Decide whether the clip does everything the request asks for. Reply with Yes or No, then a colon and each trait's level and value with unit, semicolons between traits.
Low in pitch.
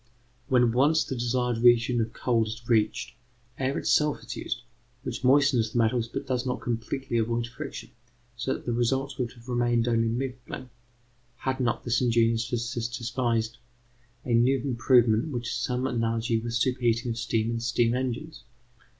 Yes: low, 120 Hz